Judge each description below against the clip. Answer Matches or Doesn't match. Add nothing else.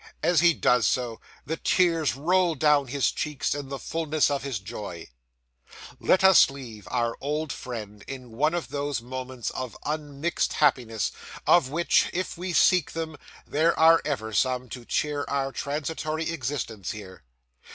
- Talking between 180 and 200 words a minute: Doesn't match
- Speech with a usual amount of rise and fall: Matches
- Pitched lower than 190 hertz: Matches